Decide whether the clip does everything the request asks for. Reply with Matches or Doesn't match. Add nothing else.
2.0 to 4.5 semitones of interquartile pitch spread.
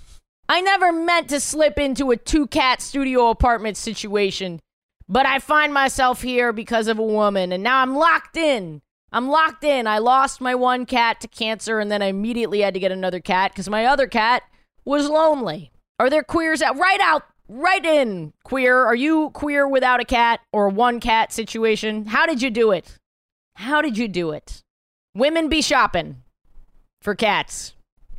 Doesn't match